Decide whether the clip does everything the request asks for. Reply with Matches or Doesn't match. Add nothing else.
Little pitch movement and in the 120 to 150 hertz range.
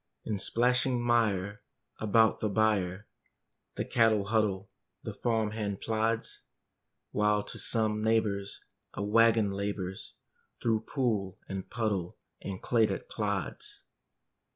Doesn't match